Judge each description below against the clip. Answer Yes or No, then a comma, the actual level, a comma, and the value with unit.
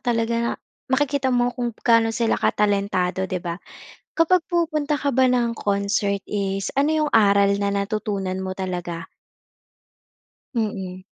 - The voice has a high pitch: Yes, high, 210 Hz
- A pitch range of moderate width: Yes, average, 4.3 semitones